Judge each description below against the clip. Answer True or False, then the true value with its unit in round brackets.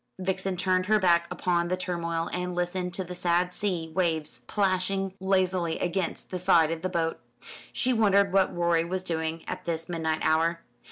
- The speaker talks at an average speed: True (175 wpm)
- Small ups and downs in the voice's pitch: True (1.9 semitones)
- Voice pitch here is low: False (180 Hz)